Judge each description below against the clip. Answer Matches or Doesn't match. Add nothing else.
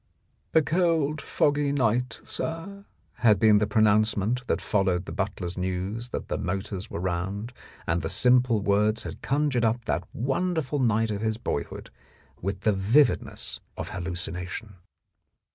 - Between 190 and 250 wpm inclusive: Doesn't match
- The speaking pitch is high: Doesn't match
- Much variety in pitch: Doesn't match